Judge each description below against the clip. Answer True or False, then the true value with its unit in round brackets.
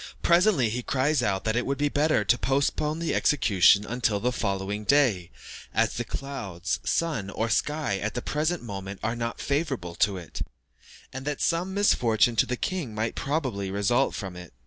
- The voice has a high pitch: False (120 Hz)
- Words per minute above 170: True (180 wpm)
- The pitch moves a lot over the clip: True (6.5 semitones)